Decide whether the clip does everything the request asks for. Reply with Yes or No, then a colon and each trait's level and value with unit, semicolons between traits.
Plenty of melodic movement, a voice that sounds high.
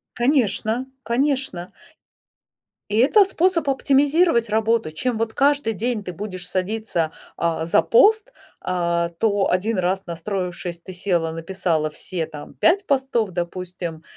Yes: wide, 6.6 semitones; high, 205 Hz